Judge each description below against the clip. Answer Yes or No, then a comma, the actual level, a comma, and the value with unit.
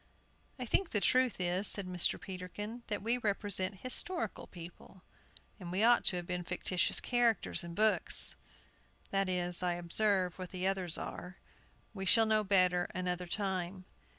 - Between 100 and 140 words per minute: No, average, 155 wpm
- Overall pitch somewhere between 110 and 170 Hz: No, high, 190 Hz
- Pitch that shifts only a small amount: No, average, 3.1 semitones